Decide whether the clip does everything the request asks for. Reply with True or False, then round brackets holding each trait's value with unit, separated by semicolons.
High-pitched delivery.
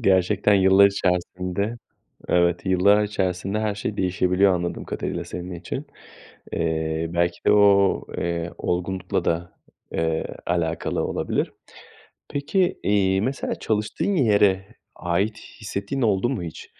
False (95 Hz)